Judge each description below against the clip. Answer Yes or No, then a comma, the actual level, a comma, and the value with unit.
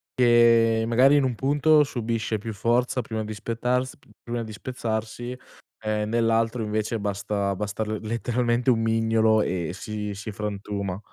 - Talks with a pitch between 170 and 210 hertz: No, low, 115 Hz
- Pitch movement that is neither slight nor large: No, narrow, 2.1 semitones